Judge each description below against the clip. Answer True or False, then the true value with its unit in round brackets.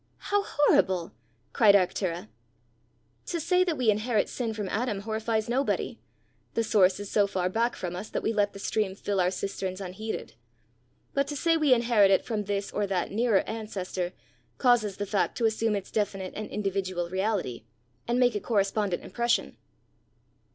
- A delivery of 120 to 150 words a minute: False (170 wpm)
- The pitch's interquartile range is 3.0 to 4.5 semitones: True (3.3 semitones)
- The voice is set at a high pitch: True (210 Hz)